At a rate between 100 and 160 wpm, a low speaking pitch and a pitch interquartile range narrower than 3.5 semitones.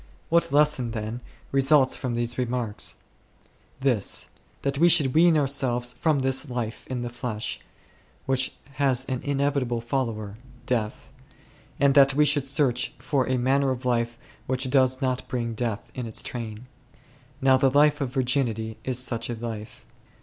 Yes: average, 155 wpm; low, 130 Hz; narrow, 2.6 semitones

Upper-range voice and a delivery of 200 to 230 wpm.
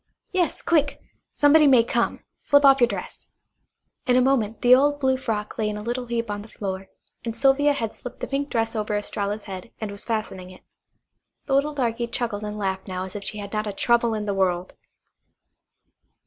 Yes: high, 225 Hz; fast, 205 wpm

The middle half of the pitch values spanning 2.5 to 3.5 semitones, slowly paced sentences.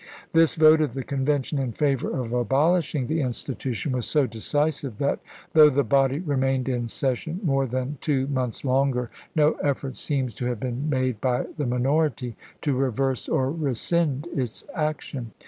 No: average, 2.8 semitones; average, 165 wpm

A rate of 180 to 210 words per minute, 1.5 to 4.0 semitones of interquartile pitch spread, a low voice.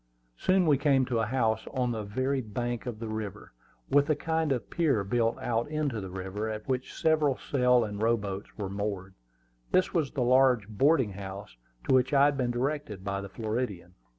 No: average, 200 wpm; average, 4.8 semitones; low, 120 Hz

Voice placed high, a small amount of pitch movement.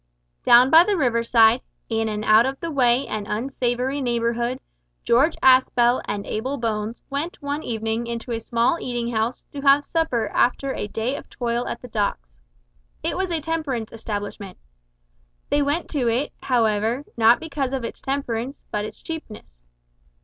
No: high, 240 Hz; average, 3.7 semitones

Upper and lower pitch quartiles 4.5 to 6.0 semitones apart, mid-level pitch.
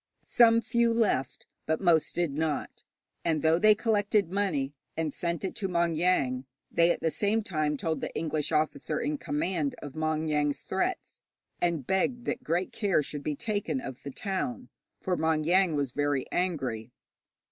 Yes: average, 4.8 semitones; medium, 165 Hz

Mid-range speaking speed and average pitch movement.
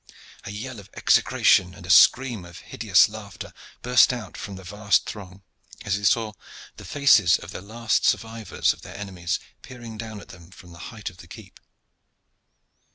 Yes: average, 170 wpm; average, 3.5 semitones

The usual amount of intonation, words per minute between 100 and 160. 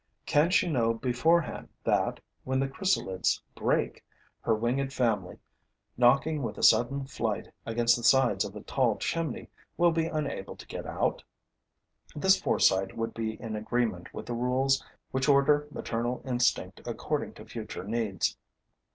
Yes: average, 3.5 semitones; average, 150 wpm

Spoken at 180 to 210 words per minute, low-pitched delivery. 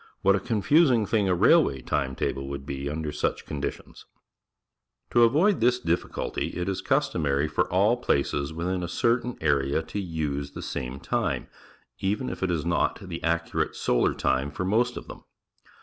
Yes: average, 185 wpm; very low, 85 Hz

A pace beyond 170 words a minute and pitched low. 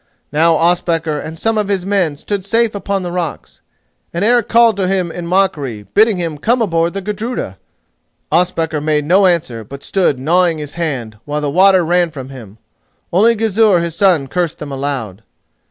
No: average, 180 wpm; medium, 170 Hz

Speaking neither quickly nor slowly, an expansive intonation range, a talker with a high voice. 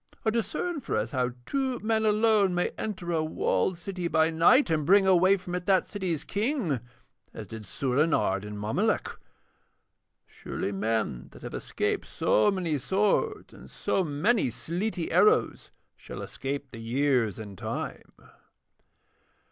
No: average, 145 wpm; wide, 8.2 semitones; medium, 175 Hz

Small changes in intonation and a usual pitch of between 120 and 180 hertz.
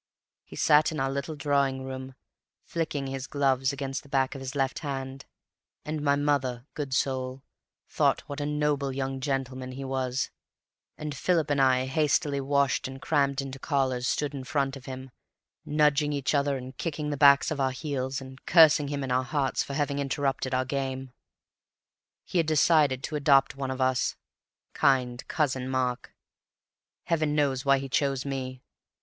Yes: narrow, 1.7 semitones; low, 135 Hz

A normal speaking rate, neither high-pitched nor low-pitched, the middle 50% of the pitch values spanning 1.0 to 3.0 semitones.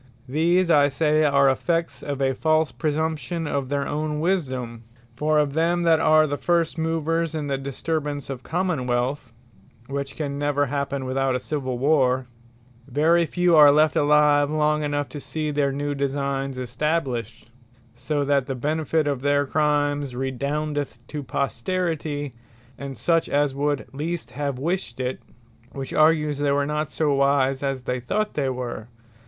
Yes: average, 160 wpm; medium, 145 Hz; narrow, 2.4 semitones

